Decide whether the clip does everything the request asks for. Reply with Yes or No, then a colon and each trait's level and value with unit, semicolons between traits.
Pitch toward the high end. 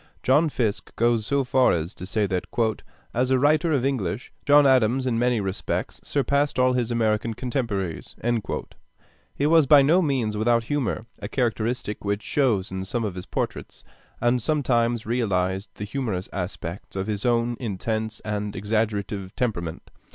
No: low, 115 Hz